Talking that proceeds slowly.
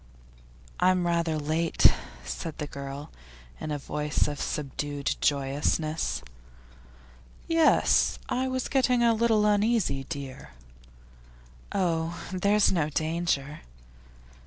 Yes: slow, 100 wpm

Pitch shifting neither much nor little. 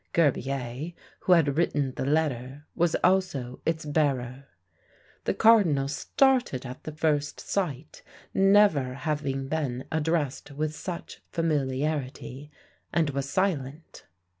Yes: average, 3.4 semitones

